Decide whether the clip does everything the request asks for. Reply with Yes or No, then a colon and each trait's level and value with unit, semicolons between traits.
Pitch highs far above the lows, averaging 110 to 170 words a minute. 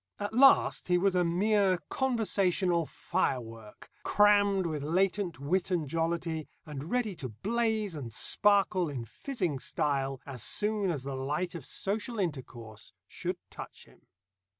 Yes: wide, 6.2 semitones; average, 140 wpm